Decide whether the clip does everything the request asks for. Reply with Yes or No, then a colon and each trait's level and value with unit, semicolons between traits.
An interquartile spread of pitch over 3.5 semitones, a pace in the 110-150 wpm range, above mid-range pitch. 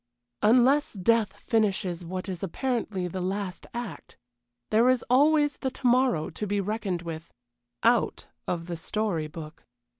Yes: average, 5.2 semitones; average, 145 wpm; high, 205 Hz